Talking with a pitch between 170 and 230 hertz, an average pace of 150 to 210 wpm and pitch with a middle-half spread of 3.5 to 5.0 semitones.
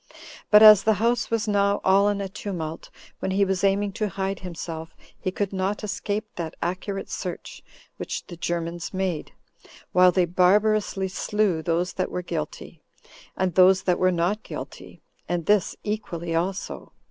No: high, 190 Hz; average, 160 wpm; average, 2.7 semitones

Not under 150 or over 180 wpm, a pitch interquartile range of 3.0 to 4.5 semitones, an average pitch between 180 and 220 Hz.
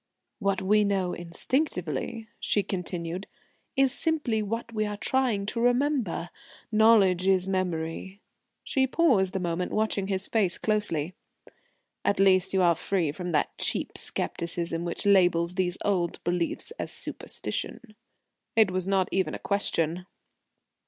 No: slow, 135 wpm; average, 3.3 semitones; high, 190 Hz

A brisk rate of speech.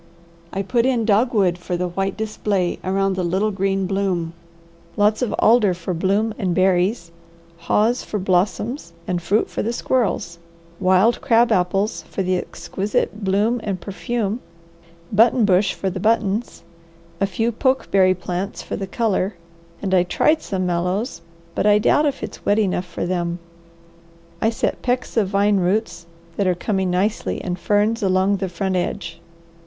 No: average, 160 wpm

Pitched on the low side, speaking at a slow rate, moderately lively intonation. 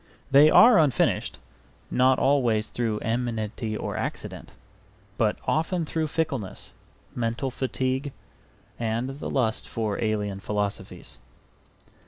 Yes: low, 120 Hz; slow, 105 wpm; average, 4.1 semitones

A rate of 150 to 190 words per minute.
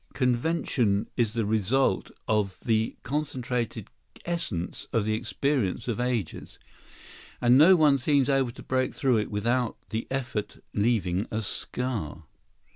No: average, 140 wpm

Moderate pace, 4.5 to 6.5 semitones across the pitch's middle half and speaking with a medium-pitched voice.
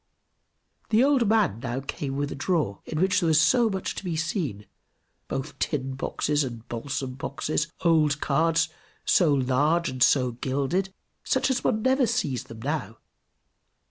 Yes: average, 155 wpm; wide, 5.5 semitones; medium, 150 Hz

